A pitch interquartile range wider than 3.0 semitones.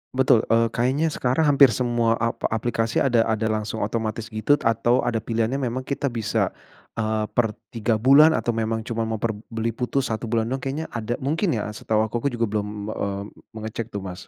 No: narrow, 2.4 semitones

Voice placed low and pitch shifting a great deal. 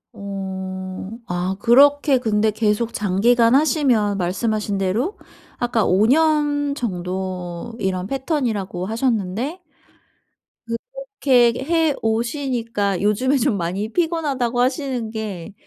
No: high, 230 Hz; wide, 5.7 semitones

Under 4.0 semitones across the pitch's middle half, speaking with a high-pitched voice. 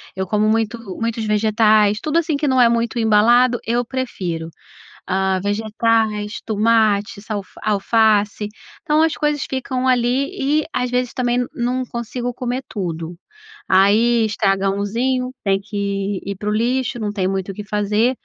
Yes: average, 3.3 semitones; high, 220 Hz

